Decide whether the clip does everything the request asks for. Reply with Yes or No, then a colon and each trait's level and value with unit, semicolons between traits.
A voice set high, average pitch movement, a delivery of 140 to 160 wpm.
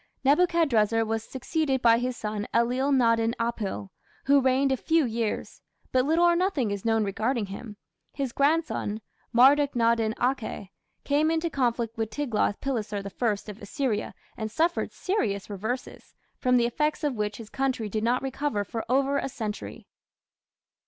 Yes: high, 240 Hz; average, 4.2 semitones; average, 155 wpm